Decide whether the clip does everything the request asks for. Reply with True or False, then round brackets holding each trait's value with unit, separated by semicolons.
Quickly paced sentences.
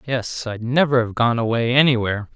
False (180 wpm)